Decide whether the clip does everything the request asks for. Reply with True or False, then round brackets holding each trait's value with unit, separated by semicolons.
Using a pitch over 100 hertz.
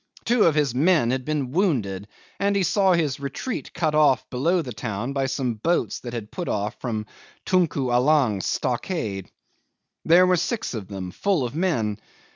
True (135 Hz)